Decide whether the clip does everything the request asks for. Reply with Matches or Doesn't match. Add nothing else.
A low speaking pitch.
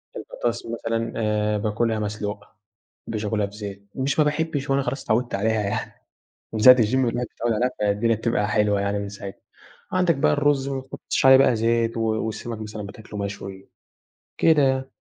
Matches